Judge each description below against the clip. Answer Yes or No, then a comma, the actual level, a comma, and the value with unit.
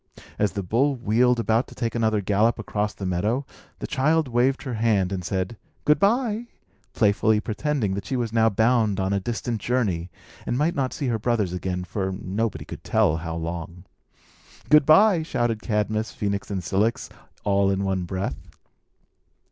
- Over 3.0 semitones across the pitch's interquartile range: Yes, average, 4.3 semitones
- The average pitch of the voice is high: No, low, 110 Hz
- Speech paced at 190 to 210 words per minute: No, average, 170 wpm